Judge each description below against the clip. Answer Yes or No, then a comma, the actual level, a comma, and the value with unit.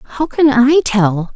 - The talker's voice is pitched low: No, very high, 250 Hz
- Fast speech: No, average, 175 wpm